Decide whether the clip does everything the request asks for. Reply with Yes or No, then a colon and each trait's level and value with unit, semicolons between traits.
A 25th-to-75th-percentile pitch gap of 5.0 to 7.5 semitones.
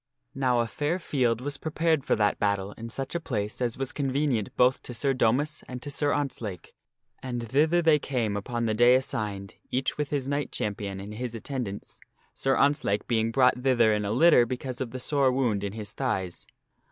No: average, 4.1 semitones